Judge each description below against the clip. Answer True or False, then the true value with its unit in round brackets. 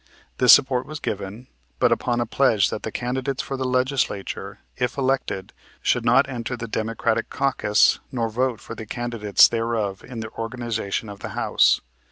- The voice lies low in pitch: True (120 Hz)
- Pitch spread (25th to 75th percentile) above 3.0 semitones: False (2.7 semitones)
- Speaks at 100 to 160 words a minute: False (170 wpm)